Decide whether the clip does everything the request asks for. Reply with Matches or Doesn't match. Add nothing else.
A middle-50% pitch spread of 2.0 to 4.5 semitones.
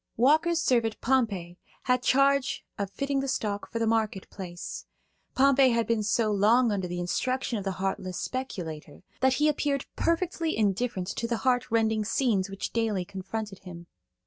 Doesn't match